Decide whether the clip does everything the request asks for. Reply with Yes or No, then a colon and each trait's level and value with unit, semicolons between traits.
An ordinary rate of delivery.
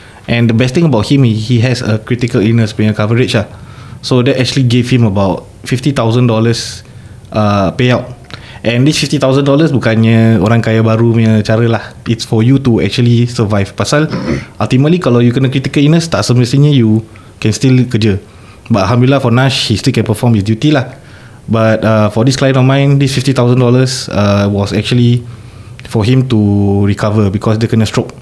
No: fast, 175 wpm